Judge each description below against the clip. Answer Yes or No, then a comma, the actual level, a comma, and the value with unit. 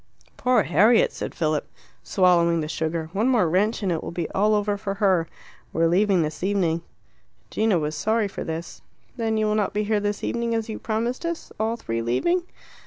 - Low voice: No, high, 200 Hz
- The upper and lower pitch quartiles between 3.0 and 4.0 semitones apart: No, average, 4.7 semitones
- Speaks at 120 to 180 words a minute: No, average, 200 wpm